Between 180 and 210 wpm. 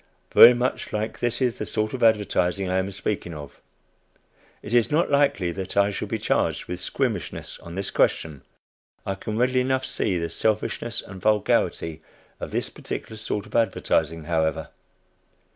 No: average, 165 wpm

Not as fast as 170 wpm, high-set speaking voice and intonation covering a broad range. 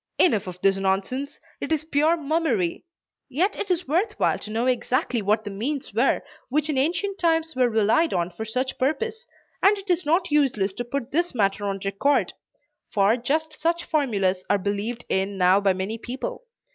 No: average, 185 wpm; very high, 255 Hz; wide, 7.9 semitones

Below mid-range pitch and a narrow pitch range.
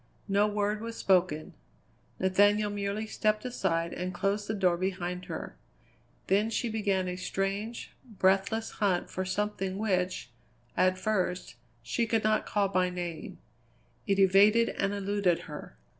No: high, 195 Hz; narrow, 2.3 semitones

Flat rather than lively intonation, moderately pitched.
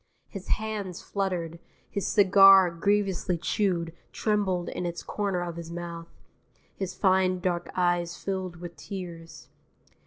Yes: narrow, 2.2 semitones; medium, 180 Hz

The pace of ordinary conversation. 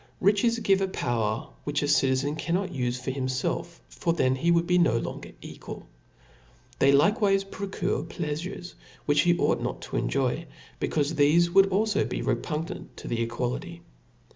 Yes: average, 165 wpm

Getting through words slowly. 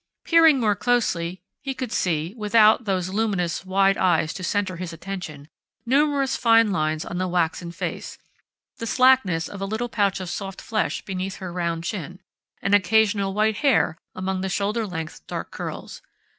No: average, 165 wpm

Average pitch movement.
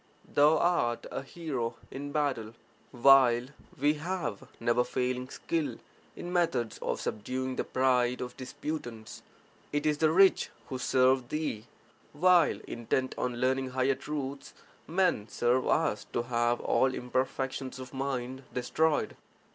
Yes: average, 3.3 semitones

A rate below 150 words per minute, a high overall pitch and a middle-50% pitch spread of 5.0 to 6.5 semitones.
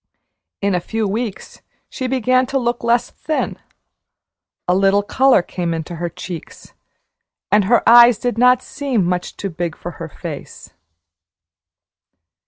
Yes: average, 140 wpm; high, 210 Hz; wide, 5.6 semitones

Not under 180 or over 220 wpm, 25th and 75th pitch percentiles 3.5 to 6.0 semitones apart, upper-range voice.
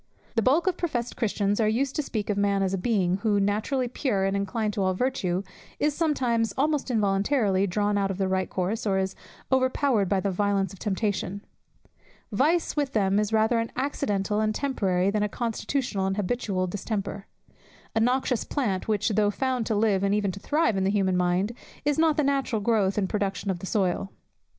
Yes: average, 200 wpm; average, 4.0 semitones; high, 210 Hz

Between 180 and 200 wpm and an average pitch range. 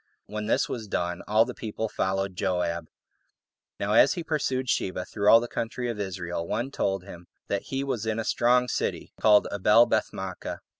Yes: average, 185 wpm; average, 3.9 semitones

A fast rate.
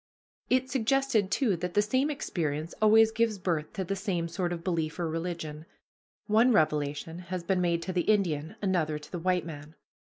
No: average, 185 wpm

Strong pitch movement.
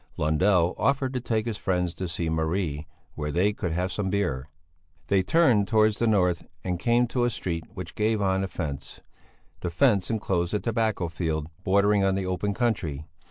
No: average, 4.2 semitones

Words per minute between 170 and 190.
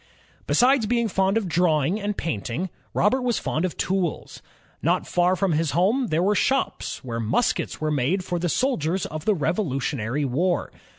Yes: average, 175 wpm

